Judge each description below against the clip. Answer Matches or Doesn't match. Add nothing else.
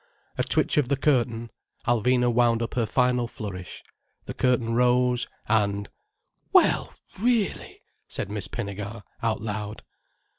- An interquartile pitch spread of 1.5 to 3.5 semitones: Matches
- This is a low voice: Matches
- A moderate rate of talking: Doesn't match